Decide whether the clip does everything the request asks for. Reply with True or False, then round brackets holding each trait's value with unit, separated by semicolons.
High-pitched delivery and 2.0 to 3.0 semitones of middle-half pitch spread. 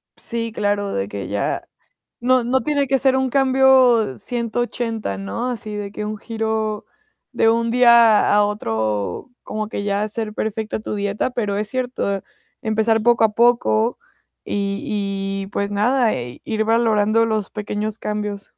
True (215 Hz; 2.6 semitones)